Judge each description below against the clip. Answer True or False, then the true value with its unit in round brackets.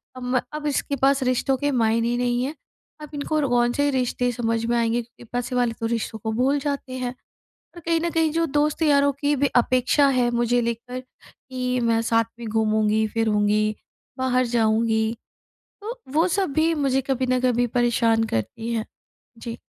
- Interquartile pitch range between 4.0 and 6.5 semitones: False (3.5 semitones)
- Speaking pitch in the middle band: False (245 Hz)